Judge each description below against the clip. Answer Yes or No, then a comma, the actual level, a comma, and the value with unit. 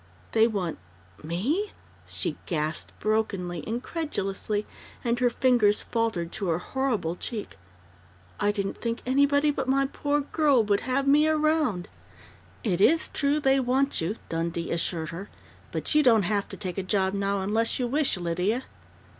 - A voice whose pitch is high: Yes, high, 220 Hz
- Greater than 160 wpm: No, average, 155 wpm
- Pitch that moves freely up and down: Yes, wide, 6.3 semitones